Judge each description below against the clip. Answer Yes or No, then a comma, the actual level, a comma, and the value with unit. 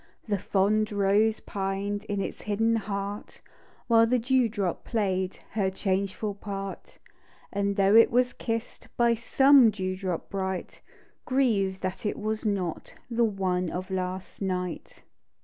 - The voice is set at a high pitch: Yes, high, 200 Hz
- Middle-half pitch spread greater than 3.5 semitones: No, average, 2.8 semitones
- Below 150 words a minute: Yes, average, 140 wpm